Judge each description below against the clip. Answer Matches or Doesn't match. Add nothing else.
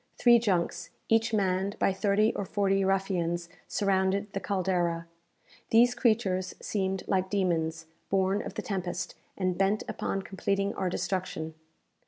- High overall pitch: Matches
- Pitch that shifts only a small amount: Matches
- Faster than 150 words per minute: Doesn't match